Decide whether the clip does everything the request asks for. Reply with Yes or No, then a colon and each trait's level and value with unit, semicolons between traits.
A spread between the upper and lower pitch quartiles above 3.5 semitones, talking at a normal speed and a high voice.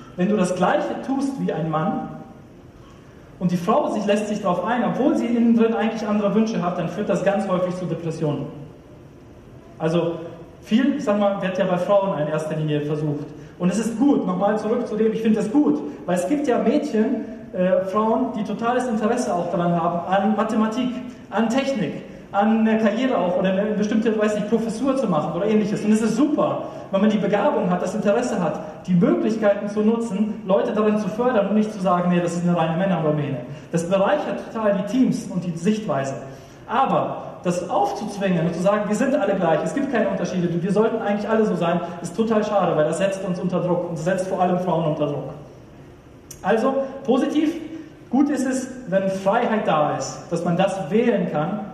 No: average, 4.0 semitones; fast, 205 wpm; high, 200 Hz